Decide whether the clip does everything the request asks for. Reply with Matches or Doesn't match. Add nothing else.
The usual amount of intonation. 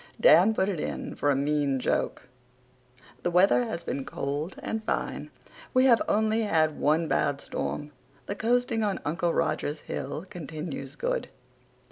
Doesn't match